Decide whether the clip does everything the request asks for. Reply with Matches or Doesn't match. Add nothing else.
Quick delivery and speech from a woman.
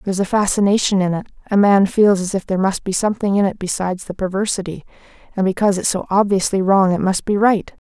Matches